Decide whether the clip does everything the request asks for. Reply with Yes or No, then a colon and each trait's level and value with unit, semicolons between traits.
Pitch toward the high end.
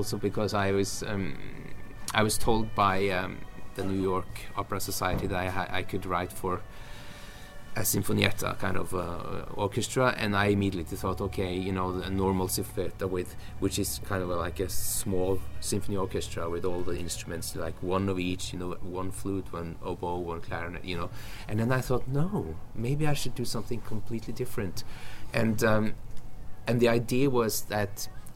No: low, 100 Hz